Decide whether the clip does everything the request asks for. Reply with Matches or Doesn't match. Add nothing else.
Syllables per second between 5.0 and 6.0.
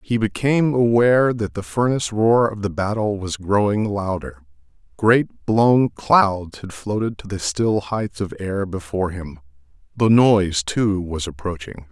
Doesn't match